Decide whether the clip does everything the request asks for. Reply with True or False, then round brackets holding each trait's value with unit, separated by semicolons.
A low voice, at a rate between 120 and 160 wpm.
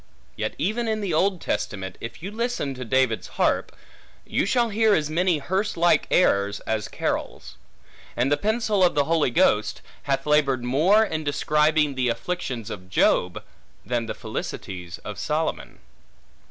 False (150 Hz; 155 wpm)